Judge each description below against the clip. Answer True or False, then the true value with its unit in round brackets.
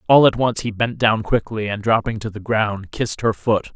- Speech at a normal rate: False (240 wpm)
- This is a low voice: True (110 Hz)